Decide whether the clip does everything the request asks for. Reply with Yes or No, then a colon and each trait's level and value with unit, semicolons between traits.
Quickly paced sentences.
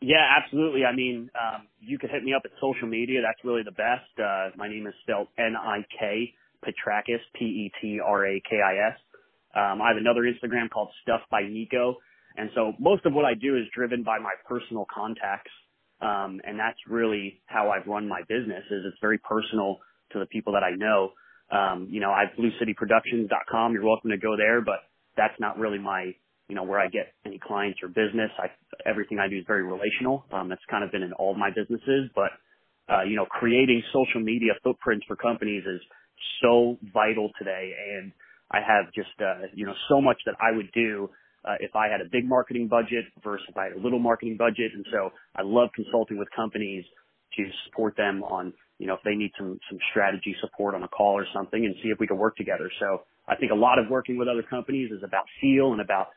Yes: fast, 220 wpm